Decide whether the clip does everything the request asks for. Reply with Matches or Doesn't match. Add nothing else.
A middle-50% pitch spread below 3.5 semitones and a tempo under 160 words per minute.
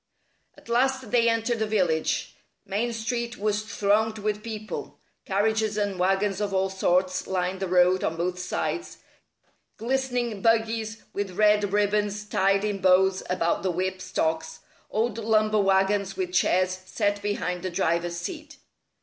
Matches